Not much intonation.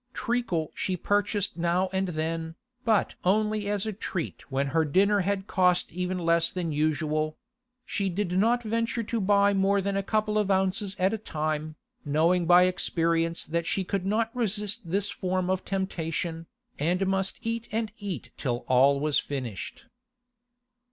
No: average, 3.8 semitones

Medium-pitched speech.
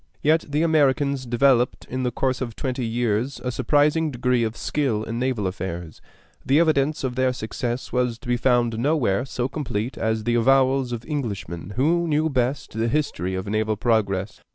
No: low, 125 Hz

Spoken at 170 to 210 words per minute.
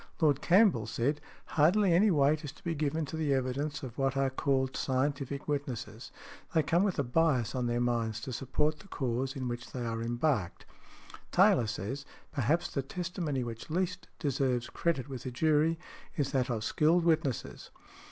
Yes: average, 175 wpm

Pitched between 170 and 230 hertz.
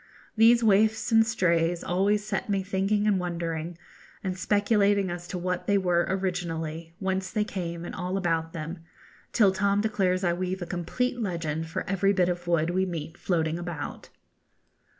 Yes: medium, 185 Hz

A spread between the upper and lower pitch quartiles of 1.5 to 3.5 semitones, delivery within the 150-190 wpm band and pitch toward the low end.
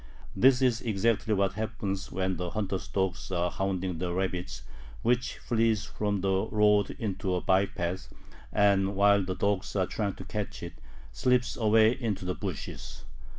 Yes: narrow, 2.6 semitones; average, 160 wpm; low, 100 Hz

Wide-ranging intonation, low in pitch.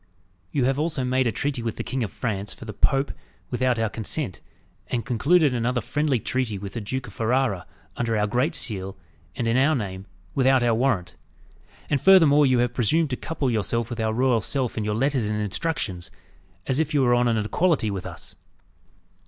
No: average, 3.8 semitones; low, 120 Hz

